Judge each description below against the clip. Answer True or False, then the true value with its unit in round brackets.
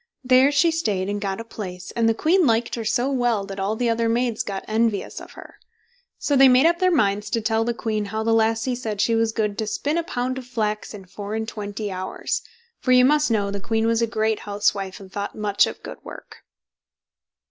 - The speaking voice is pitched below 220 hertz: False (225 Hz)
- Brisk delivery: True (230 wpm)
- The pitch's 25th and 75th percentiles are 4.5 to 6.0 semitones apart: False (3.2 semitones)